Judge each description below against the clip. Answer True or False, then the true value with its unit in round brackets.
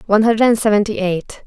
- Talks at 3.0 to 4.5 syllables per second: False (6.1 syllables/s)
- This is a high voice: True (210 Hz)